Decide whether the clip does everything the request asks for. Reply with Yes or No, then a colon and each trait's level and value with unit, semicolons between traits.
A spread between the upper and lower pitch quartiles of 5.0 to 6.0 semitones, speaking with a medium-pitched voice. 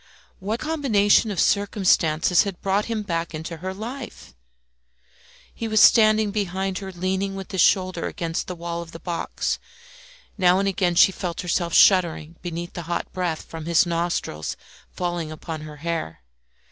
No: average, 2.9 semitones; medium, 180 Hz